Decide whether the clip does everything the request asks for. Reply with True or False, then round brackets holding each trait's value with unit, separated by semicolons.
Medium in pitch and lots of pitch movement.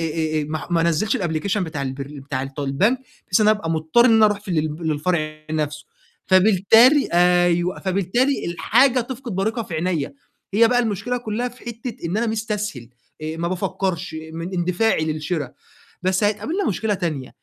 True (180 Hz; 5.7 semitones)